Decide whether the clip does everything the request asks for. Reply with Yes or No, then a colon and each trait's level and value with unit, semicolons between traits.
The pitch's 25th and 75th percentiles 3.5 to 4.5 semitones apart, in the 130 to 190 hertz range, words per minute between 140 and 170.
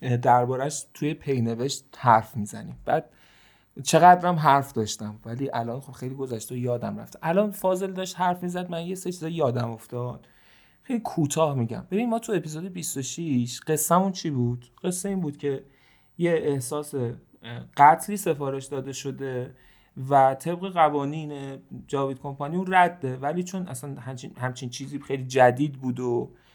No: average, 5.2 semitones; medium, 140 Hz; average, 150 wpm